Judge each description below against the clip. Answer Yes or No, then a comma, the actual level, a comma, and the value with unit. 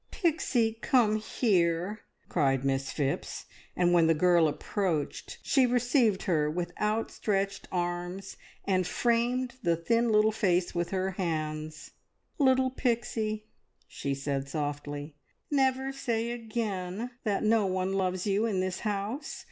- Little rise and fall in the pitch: No, average, 5.1 semitones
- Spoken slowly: Yes, slow, 130 wpm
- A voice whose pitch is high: Yes, high, 195 Hz